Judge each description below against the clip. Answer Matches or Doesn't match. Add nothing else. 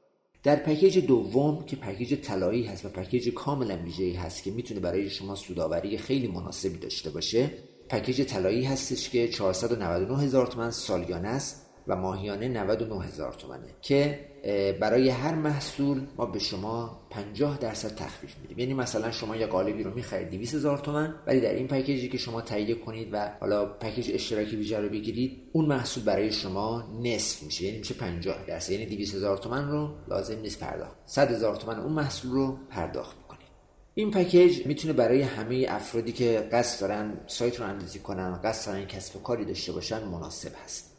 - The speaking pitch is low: Matches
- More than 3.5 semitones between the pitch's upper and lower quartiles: Matches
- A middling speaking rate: Doesn't match